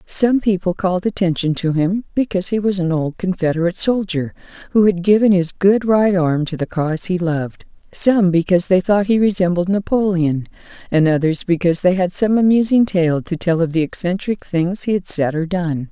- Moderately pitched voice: Yes, medium, 180 Hz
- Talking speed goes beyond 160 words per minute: Yes, average, 190 wpm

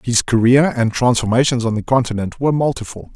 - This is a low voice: Yes, low, 120 Hz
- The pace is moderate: Yes, average, 170 wpm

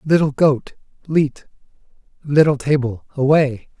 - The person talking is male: Yes, male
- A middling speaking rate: No, slow, 95 wpm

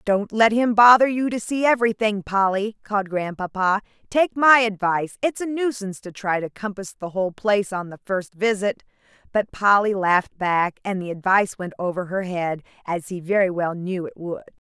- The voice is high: Yes, high, 200 Hz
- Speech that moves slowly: No, average, 185 wpm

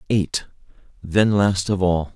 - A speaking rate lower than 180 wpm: Yes, average, 140 wpm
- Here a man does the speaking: Yes, male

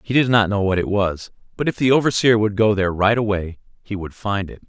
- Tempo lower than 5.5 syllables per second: No, 5.9 syllables/s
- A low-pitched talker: Yes, low, 105 Hz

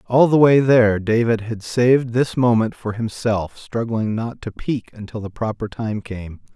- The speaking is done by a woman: No, male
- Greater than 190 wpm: No, average, 185 wpm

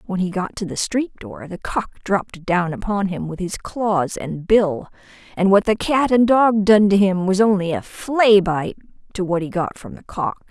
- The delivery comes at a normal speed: No, fast, 225 wpm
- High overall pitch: Yes, high, 195 Hz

